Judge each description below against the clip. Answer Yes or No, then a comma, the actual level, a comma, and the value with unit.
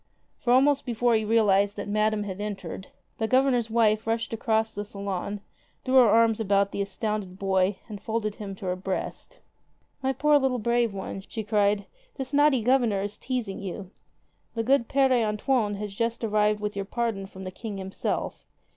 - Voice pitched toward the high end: Yes, high, 215 Hz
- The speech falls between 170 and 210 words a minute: Yes, average, 180 wpm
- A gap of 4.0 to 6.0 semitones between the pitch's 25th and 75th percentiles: No, average, 2.9 semitones